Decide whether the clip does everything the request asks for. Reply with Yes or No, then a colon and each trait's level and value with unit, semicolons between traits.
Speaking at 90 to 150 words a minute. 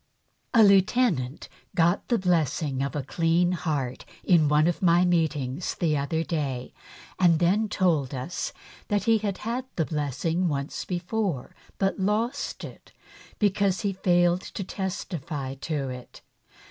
Yes: average, 140 wpm